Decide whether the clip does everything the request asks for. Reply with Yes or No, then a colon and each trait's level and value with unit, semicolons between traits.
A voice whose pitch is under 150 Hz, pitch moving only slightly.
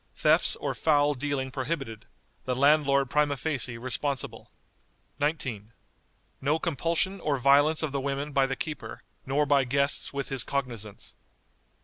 Yes: medium, 140 Hz; narrow, 2.1 semitones